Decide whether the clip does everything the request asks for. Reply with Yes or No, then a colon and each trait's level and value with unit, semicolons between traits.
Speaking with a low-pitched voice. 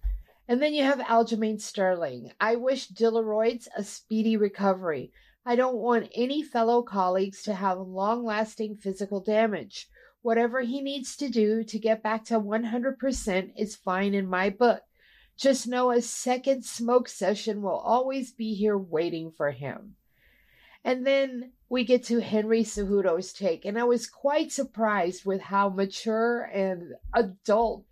No: high, 220 Hz